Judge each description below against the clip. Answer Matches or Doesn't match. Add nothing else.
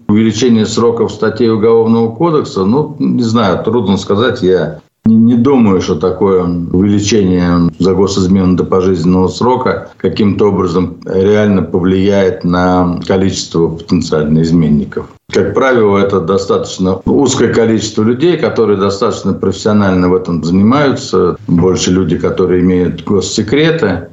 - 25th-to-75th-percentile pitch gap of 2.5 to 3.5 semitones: Matches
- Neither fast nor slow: Matches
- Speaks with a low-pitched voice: Matches